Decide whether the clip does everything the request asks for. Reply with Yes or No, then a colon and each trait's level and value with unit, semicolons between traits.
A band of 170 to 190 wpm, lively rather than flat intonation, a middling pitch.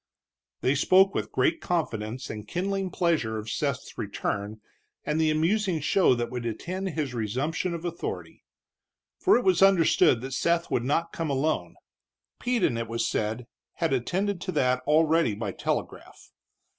No: average, 155 wpm; wide, 7.0 semitones; medium, 155 Hz